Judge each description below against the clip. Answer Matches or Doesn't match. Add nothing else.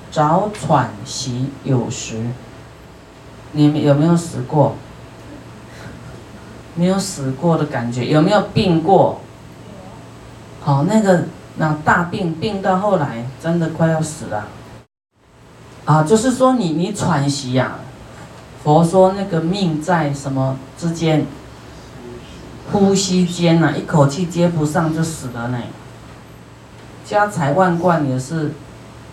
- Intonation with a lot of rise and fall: Doesn't match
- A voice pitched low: Doesn't match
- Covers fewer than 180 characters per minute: Matches